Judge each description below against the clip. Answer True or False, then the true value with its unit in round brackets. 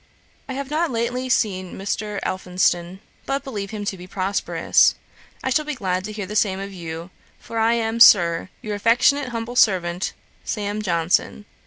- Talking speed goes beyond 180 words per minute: False (170 wpm)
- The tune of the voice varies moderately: True (4.0 semitones)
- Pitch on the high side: True (205 Hz)